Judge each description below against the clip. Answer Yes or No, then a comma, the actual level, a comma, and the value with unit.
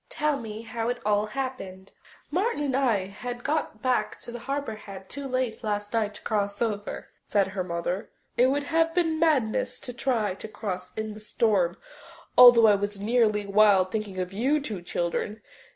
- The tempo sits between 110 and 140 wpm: No, average, 175 wpm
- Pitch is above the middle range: Yes, high, 220 Hz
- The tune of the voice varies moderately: Yes, average, 4.2 semitones